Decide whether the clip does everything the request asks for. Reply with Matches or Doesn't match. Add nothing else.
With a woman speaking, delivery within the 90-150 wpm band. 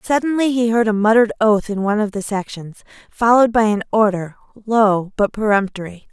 Doesn't match